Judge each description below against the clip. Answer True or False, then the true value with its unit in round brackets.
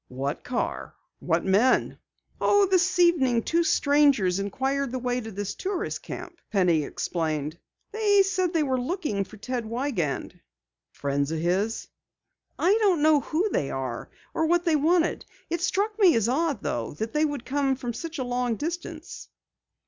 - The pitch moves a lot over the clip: True (8.8 semitones)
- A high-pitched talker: True (265 Hz)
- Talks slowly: False (165 wpm)